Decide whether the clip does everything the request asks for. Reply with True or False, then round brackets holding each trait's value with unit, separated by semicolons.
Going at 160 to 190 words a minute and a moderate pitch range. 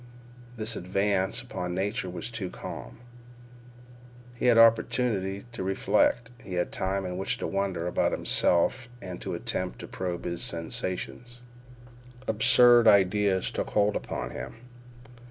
False (135 wpm; 3.9 semitones)